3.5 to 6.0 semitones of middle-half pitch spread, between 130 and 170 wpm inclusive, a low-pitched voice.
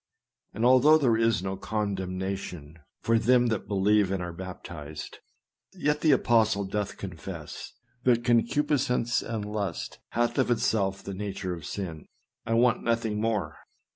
Yes: average, 3.9 semitones; average, 140 wpm; low, 105 Hz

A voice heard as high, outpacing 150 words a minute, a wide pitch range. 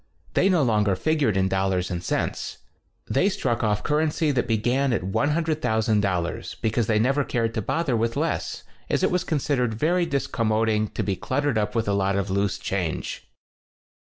No: low, 115 Hz; average, 180 wpm; wide, 5.9 semitones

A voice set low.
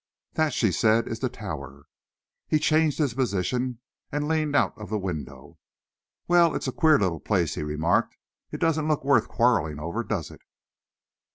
Yes: low, 115 Hz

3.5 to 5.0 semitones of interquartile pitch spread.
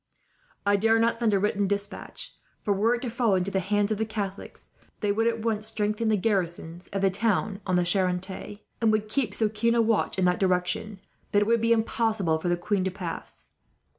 No: average, 2.8 semitones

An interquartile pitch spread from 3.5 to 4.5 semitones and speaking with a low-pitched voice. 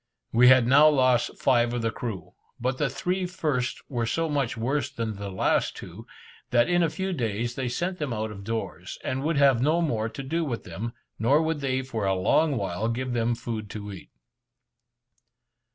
Yes: average, 4.2 semitones; low, 125 Hz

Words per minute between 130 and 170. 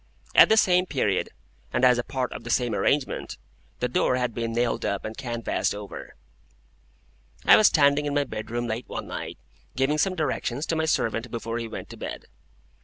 No: average, 185 wpm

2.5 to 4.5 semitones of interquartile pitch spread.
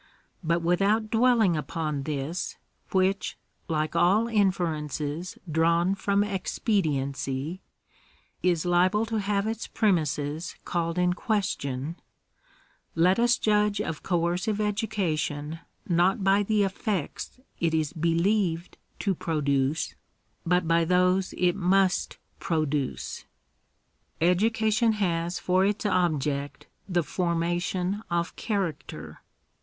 Yes: average, 3.6 semitones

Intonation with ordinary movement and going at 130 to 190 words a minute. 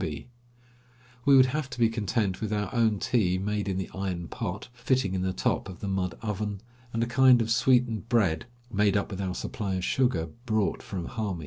No: average, 3.9 semitones; fast, 205 wpm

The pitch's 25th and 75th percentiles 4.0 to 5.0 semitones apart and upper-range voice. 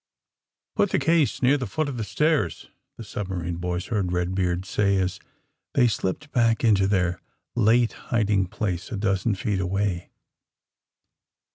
No: average, 4.3 semitones; low, 100 Hz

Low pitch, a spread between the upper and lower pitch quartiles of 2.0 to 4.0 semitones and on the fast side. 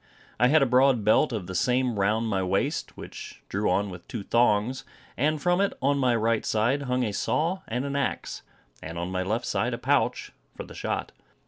No: low, 120 Hz; average, 5.1 semitones; fast, 210 wpm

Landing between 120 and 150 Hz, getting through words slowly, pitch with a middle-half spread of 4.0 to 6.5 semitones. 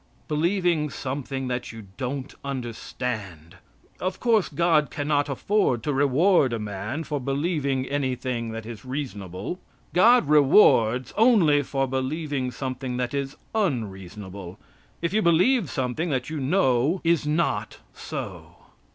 Yes: low, 135 Hz; slow, 125 wpm; average, 4.5 semitones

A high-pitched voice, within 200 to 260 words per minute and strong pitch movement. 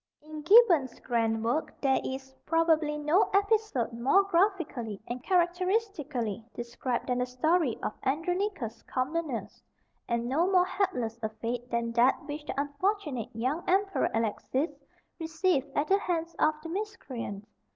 No: very high, 295 Hz; average, 140 wpm; wide, 6.7 semitones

